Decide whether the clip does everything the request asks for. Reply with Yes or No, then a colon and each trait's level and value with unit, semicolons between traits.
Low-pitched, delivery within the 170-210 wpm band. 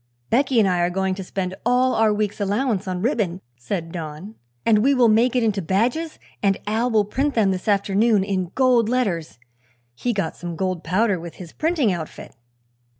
No: high, 205 Hz; average, 190 wpm